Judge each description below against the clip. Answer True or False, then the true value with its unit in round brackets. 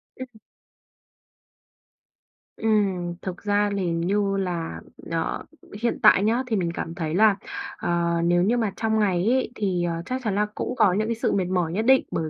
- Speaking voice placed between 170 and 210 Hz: True (195 Hz)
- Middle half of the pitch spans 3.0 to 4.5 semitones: True (3.9 semitones)